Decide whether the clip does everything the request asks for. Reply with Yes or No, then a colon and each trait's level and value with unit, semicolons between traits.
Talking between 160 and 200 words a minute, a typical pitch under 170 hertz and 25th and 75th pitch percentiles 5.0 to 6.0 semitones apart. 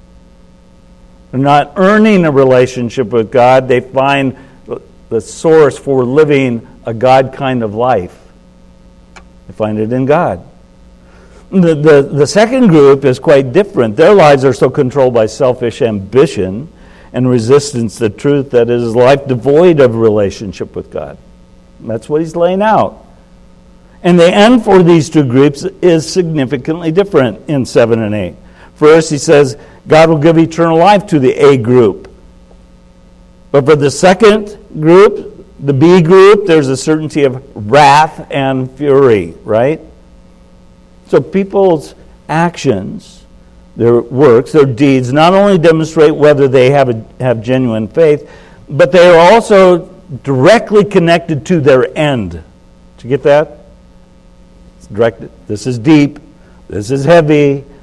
No: average, 140 wpm; medium, 140 Hz; wide, 5.6 semitones